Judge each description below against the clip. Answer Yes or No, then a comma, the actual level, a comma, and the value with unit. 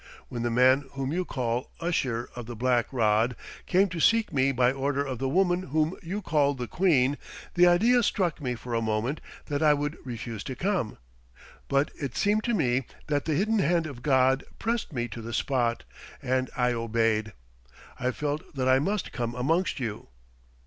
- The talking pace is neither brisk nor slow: Yes, average, 190 wpm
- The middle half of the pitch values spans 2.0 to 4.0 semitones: No, average, 5.2 semitones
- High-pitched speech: No, low, 135 Hz